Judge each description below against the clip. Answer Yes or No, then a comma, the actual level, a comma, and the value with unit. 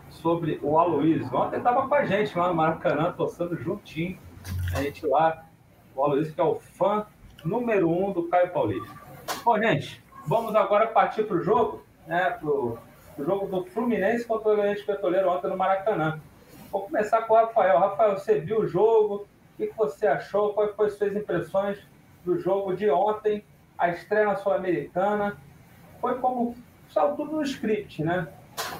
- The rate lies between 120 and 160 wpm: No, average, 170 wpm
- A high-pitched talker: Yes, high, 195 Hz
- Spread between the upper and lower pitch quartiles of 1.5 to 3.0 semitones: No, average, 4.4 semitones